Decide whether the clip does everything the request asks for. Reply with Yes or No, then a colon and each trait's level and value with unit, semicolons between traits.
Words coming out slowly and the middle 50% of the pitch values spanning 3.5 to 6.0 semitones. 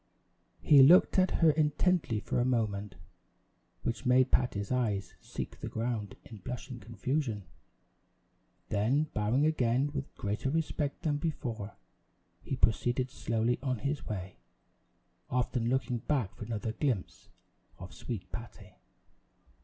Yes: slow, 125 wpm; average, 4.4 semitones